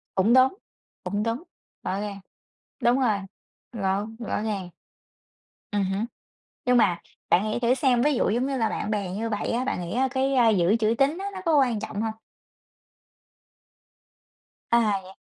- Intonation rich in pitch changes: No, average, 4.0 semitones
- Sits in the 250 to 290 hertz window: No, high, 225 Hz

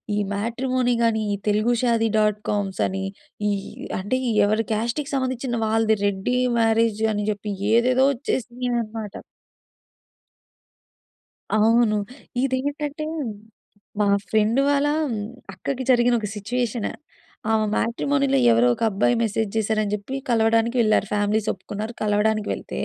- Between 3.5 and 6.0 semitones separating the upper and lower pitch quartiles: No, average, 2.7 semitones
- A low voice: No, high, 220 Hz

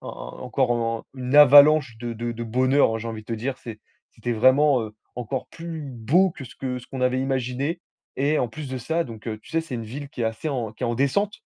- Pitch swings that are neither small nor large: Yes, average, 3.5 semitones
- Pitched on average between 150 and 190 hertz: No, low, 130 Hz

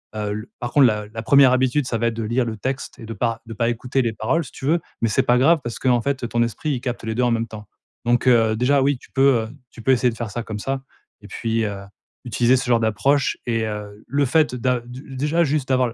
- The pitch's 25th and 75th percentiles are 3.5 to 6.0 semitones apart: No, average, 2.8 semitones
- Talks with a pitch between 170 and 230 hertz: No, low, 120 Hz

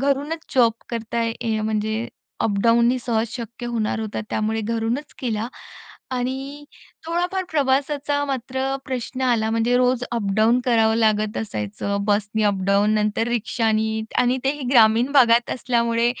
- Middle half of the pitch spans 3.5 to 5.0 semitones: No, average, 2.8 semitones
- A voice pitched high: Yes, high, 230 Hz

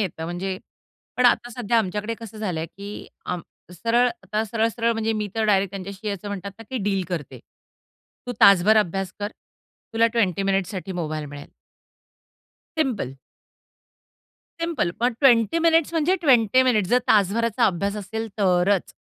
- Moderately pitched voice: No, high, 210 Hz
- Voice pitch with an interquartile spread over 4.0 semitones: No, average, 3.4 semitones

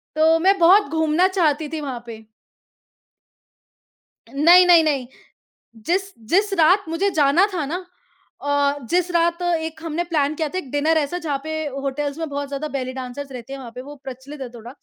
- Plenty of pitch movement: No, average, 3.6 semitones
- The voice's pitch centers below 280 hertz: No, very high, 305 Hz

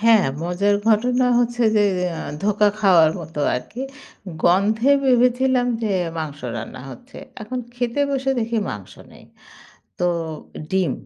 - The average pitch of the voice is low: No, high, 215 Hz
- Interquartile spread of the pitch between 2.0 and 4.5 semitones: No, wide, 5.6 semitones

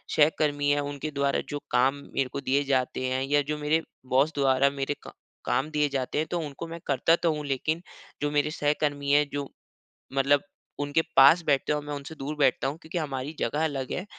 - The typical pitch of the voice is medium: Yes, medium, 145 Hz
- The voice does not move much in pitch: Yes, narrow, 1.7 semitones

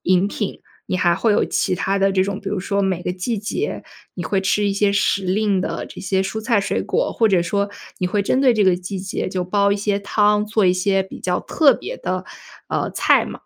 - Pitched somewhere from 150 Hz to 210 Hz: Yes, high, 200 Hz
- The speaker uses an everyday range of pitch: No, narrow, 1.9 semitones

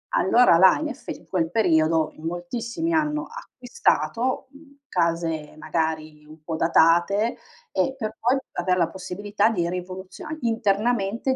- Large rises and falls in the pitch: Yes, wide, 6.4 semitones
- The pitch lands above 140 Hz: Yes, high, 190 Hz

